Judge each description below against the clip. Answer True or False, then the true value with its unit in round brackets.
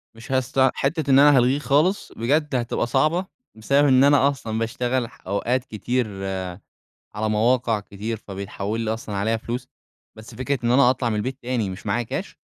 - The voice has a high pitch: False (125 Hz)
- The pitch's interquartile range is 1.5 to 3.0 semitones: False (3.4 semitones)